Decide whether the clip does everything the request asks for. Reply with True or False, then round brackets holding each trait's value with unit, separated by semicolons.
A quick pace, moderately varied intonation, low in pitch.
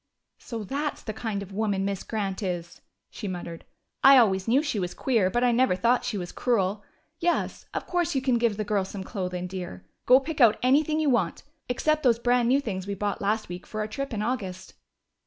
False (215 wpm; 4.8 semitones; 215 Hz)